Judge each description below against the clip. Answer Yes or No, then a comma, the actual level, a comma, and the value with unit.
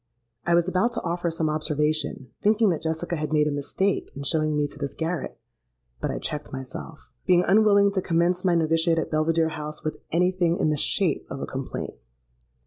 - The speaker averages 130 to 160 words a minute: No, average, 195 wpm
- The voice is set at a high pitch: No, medium, 160 Hz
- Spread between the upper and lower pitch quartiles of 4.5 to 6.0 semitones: No, average, 2.9 semitones